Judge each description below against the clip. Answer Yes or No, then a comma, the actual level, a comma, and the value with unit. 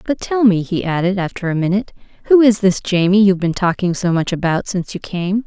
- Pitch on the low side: No, high, 190 Hz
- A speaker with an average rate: No, fast, 230 wpm